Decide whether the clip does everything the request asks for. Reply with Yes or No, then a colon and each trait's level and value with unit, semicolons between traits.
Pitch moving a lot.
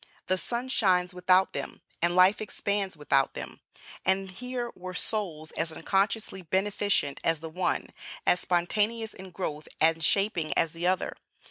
No: average, 3.4 semitones